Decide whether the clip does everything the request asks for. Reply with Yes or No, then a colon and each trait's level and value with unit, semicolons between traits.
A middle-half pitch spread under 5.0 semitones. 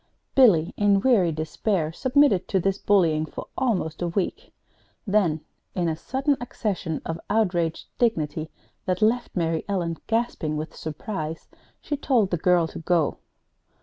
No: average, 5.3 semitones